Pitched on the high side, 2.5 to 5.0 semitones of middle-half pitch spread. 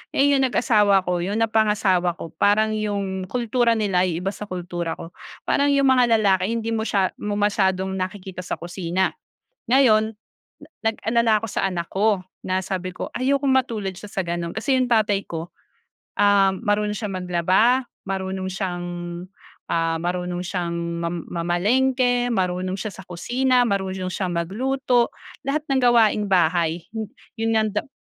Yes: high, 200 Hz; average, 3.9 semitones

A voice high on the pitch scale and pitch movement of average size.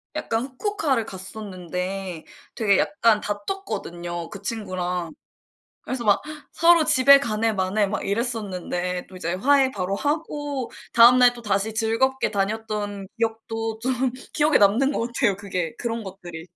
Yes: high, 220 Hz; average, 4.5 semitones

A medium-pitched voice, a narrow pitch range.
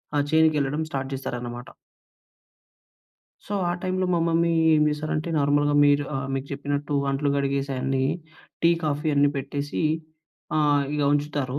Yes: medium, 145 Hz; narrow, 1.7 semitones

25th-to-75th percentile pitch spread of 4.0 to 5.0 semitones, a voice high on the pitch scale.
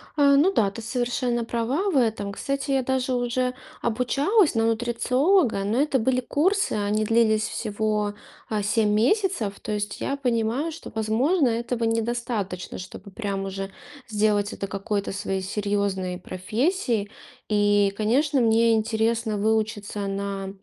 No: average, 3.6 semitones; high, 225 Hz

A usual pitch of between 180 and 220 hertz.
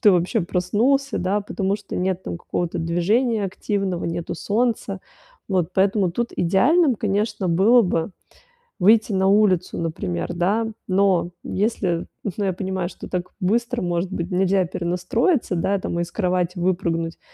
Yes: high, 190 Hz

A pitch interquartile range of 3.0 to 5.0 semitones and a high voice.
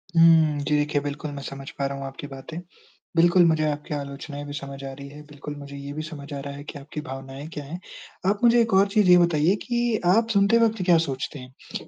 No: average, 3.6 semitones; medium, 150 Hz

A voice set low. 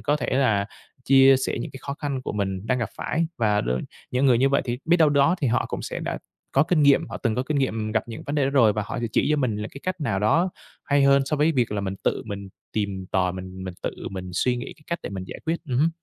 Yes: low, 125 Hz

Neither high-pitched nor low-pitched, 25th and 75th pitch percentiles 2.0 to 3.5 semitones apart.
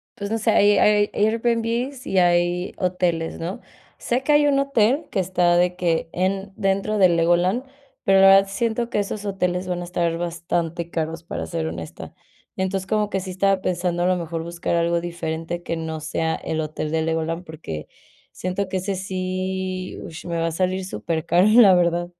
Yes: medium, 180 Hz; narrow, 2.6 semitones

